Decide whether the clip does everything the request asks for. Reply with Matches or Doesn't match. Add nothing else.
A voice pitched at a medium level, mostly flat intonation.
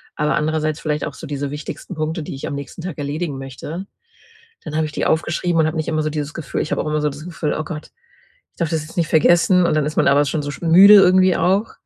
Matches